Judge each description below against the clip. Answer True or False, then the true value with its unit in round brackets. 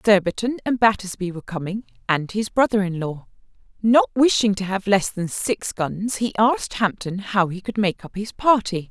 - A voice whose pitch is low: False (205 Hz)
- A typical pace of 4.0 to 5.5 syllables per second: True (4.9 syllables/s)